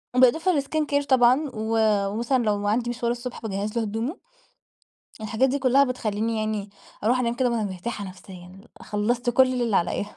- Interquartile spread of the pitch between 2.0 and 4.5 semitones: Yes, average, 3.2 semitones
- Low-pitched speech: No, high, 235 Hz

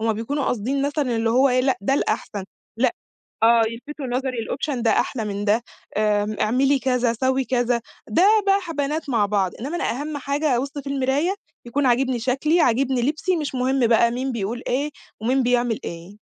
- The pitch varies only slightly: No, average, 3.4 semitones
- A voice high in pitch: Yes, very high, 255 Hz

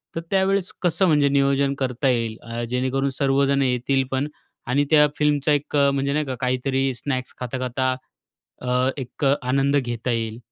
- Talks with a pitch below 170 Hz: Yes, low, 135 Hz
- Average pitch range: No, narrow, 2.0 semitones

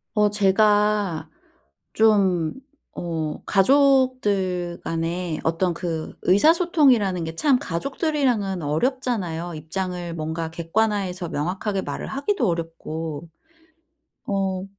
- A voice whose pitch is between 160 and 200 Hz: Yes, high, 190 Hz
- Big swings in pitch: No, average, 4.6 semitones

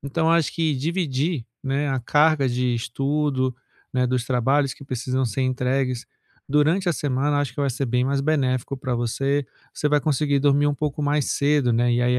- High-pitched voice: No, low, 135 Hz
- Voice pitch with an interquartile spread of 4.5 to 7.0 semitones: No, narrow, 2.5 semitones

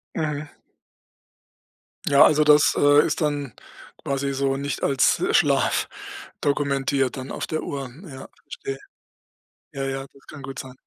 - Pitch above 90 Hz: Yes, medium, 140 Hz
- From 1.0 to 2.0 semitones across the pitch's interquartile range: Yes, narrow, 1.3 semitones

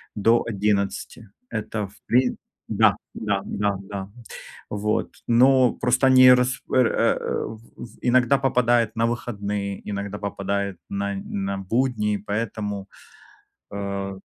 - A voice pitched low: Yes, low, 105 Hz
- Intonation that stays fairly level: No, average, 3.3 semitones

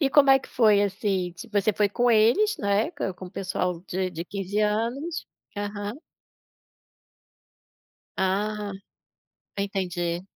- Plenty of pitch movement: No, average, 2.7 semitones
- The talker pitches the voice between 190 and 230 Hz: Yes, high, 205 Hz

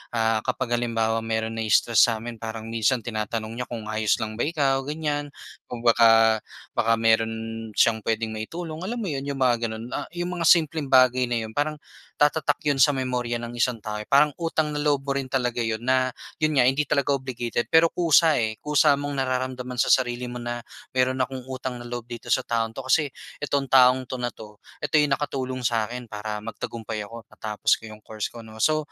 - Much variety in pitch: No, average, 3.5 semitones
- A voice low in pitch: Yes, low, 120 Hz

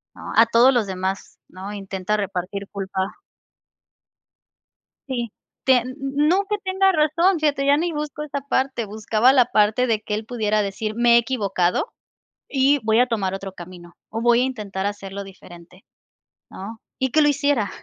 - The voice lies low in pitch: No, high, 225 Hz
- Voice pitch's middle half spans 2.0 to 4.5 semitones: No, wide, 5.6 semitones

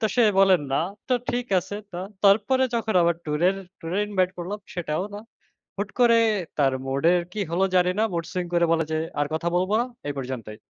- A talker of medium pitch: Yes, medium, 180 Hz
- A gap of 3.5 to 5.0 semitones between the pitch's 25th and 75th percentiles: Yes, average, 4.1 semitones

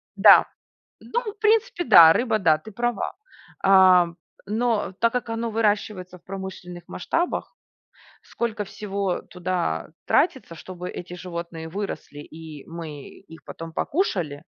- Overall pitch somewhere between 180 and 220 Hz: Yes, high, 190 Hz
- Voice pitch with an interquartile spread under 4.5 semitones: No, average, 5.1 semitones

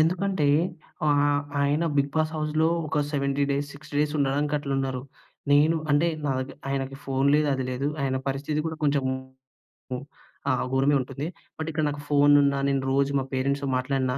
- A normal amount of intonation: No, narrow, 1.7 semitones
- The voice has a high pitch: No, medium, 140 Hz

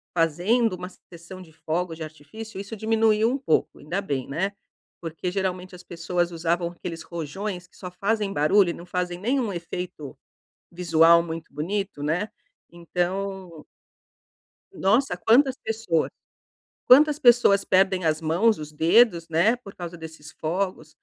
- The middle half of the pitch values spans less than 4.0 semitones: Yes, average, 3.6 semitones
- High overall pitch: No, medium, 180 Hz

